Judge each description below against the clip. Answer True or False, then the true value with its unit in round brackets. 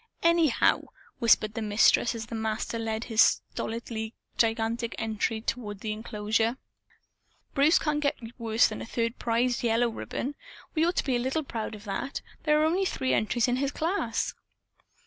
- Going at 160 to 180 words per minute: True (165 wpm)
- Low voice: False (230 Hz)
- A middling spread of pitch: True (3.2 semitones)